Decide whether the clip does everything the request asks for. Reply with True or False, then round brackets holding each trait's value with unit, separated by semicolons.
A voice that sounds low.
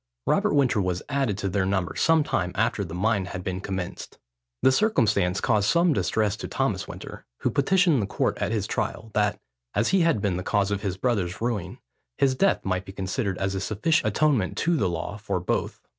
True (100 Hz)